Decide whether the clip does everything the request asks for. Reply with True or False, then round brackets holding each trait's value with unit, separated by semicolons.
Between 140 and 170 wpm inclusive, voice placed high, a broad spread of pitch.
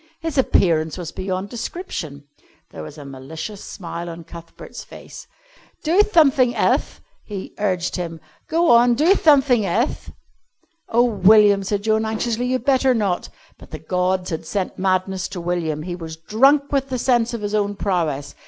True (160 wpm; 200 Hz; 6.1 semitones)